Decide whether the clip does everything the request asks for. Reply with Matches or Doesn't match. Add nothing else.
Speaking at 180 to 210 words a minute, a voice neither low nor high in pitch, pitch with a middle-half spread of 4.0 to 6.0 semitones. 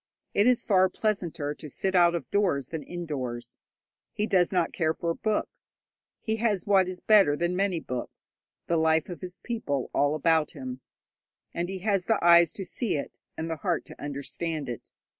Matches